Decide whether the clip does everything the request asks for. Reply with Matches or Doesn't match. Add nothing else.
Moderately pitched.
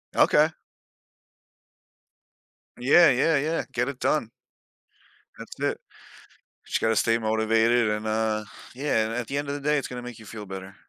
Doesn't match